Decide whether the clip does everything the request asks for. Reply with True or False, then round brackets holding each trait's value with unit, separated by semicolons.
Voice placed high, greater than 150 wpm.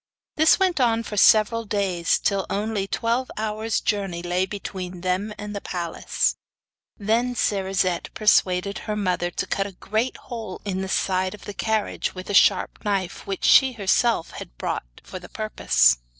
True (200 Hz; 165 wpm)